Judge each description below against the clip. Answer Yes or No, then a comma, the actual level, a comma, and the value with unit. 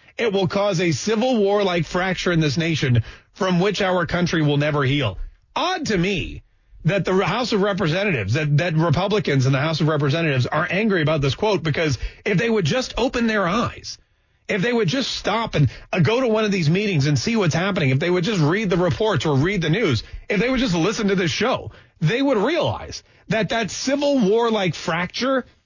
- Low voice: No, medium, 180 Hz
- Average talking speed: No, fast, 215 wpm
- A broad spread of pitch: Yes, wide, 5.9 semitones